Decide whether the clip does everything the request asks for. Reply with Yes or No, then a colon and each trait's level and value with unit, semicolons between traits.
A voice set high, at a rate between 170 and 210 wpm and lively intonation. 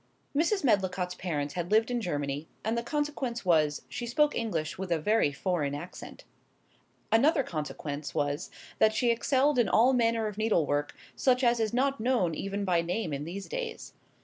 Yes: high, 210 Hz; average, 175 wpm; wide, 6.8 semitones